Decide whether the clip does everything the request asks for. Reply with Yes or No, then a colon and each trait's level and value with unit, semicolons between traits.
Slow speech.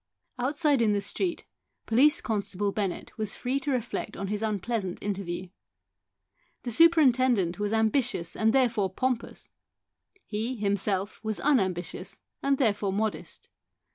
Yes: slow, 125 wpm